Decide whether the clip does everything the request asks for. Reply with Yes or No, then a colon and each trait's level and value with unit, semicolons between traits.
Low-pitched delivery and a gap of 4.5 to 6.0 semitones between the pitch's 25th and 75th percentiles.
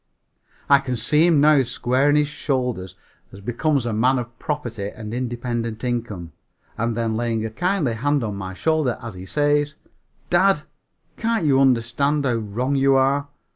No: low, 125 Hz; average, 4.1 semitones